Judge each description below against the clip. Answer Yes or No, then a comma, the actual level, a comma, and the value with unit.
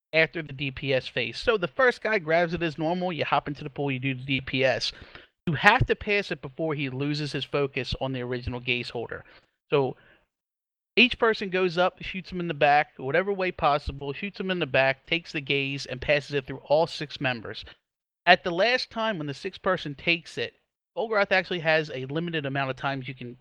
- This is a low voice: No, medium, 155 Hz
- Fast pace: Yes, fast, 215 wpm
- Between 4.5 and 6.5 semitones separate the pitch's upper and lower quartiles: Yes, average, 4.9 semitones